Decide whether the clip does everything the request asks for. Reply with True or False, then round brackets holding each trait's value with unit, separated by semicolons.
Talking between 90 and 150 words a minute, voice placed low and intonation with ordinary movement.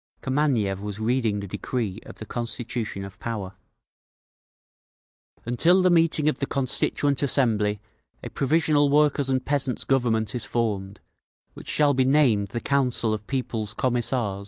True (140 wpm; 120 Hz; 4.6 semitones)